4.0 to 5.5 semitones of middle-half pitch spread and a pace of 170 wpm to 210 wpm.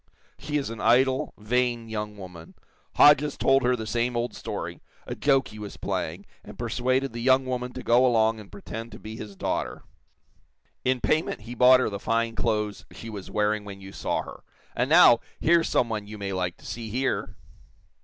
No: average, 3.2 semitones; average, 195 wpm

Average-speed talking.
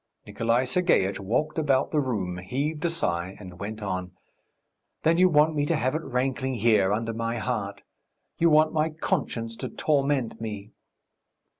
Yes: average, 160 wpm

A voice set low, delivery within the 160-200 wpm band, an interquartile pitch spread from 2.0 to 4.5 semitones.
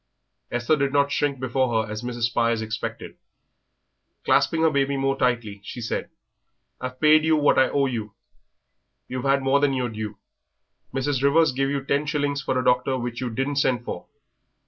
Yes: low, 130 Hz; average, 180 wpm; average, 2.7 semitones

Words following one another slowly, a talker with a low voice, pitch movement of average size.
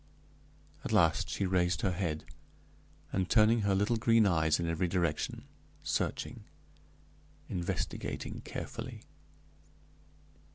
Yes: slow, 100 wpm; very low, 95 Hz; average, 3.7 semitones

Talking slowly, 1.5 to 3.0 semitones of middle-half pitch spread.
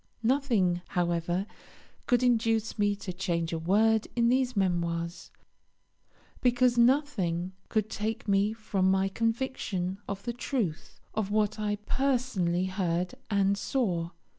No: slow, 125 wpm; average, 4.8 semitones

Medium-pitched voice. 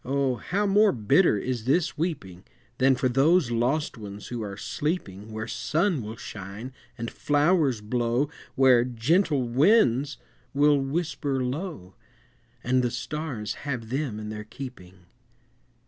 No: low, 130 Hz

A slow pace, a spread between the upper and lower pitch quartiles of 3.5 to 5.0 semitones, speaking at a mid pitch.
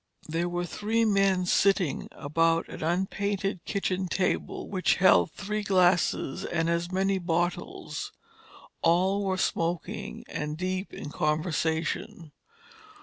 No: slow, 115 wpm; average, 2.7 semitones; medium, 180 Hz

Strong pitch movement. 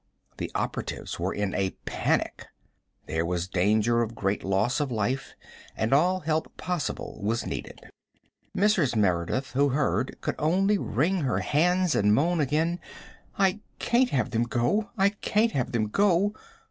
Yes: wide, 8.7 semitones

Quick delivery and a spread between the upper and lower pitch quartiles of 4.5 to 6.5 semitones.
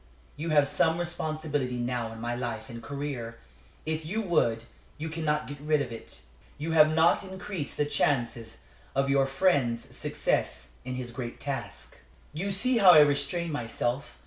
No: average, 165 wpm; average, 4.8 semitones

